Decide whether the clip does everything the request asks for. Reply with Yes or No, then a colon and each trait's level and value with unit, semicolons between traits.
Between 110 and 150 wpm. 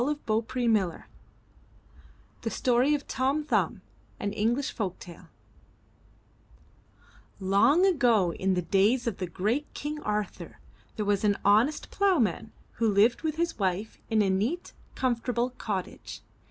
Yes: average, 140 wpm